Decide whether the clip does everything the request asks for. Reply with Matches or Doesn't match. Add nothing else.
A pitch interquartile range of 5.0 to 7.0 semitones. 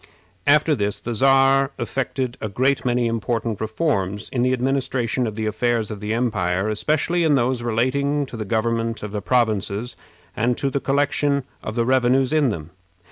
Doesn't match